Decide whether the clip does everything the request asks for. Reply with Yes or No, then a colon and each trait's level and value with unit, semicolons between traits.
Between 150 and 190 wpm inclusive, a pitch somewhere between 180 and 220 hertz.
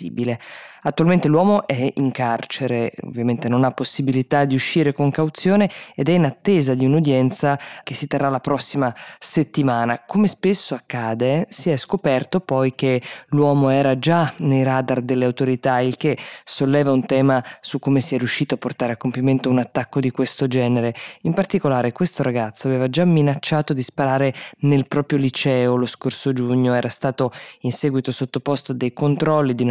No: average, 165 wpm; low, 135 Hz